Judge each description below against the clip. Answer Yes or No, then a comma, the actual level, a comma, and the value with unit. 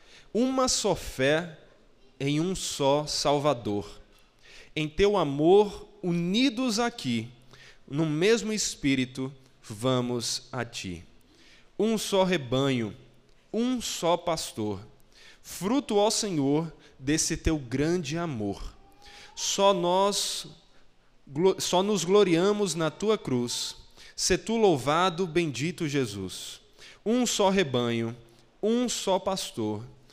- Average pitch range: No, wide, 7.4 semitones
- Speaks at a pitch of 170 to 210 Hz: No, medium, 160 Hz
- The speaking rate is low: Yes, slow, 100 wpm